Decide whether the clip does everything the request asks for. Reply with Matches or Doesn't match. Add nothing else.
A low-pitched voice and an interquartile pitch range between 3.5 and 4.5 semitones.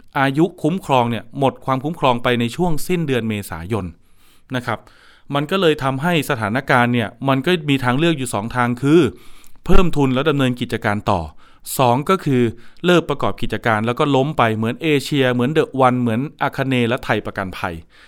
Matches